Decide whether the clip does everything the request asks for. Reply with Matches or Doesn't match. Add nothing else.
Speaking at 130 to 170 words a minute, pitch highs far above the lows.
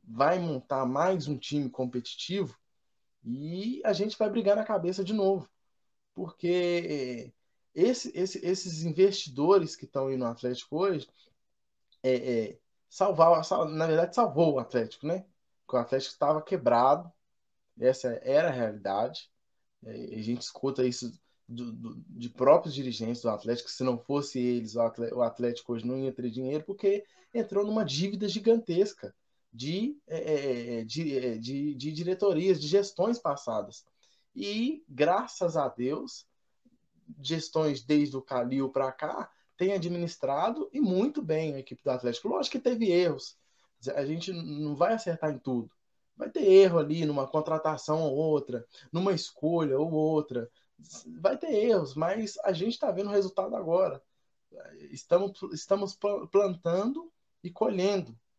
Matches